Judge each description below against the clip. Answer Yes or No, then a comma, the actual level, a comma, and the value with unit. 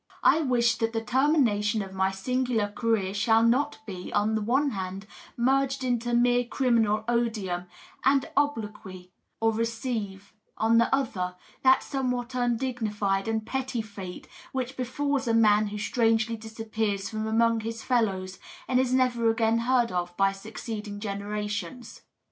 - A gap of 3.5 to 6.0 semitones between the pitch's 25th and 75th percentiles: No, average, 3.1 semitones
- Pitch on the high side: Yes, high, 225 Hz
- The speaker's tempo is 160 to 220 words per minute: No, average, 145 wpm